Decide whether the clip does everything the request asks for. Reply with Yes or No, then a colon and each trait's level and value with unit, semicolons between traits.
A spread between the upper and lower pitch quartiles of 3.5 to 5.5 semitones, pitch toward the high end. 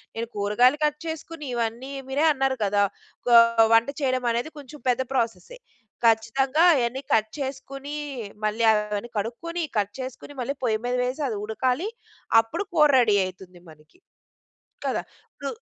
Yes: average, 3.8 semitones; very high, 250 Hz